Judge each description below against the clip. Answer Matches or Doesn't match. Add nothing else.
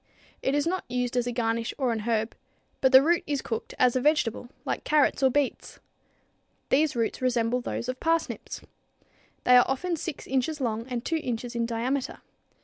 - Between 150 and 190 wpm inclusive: Matches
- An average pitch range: Matches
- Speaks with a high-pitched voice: Matches